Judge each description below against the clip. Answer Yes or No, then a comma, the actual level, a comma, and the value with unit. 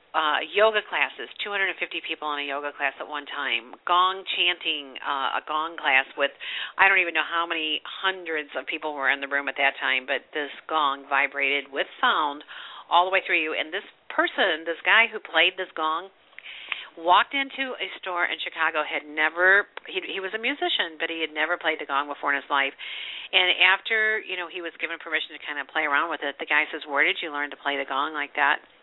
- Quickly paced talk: Yes, fast, 225 wpm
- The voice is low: No, medium, 160 Hz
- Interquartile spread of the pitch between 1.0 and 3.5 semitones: No, average, 4.3 semitones